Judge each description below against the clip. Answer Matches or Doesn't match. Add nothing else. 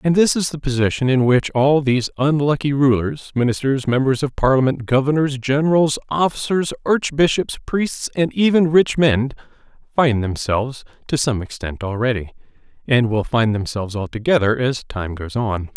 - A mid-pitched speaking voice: Doesn't match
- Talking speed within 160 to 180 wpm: Doesn't match